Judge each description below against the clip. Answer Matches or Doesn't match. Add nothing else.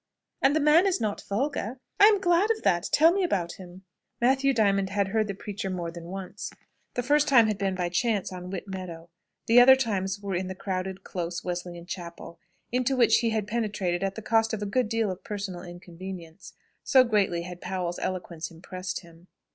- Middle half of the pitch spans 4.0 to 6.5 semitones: Matches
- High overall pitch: Matches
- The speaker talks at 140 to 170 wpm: Doesn't match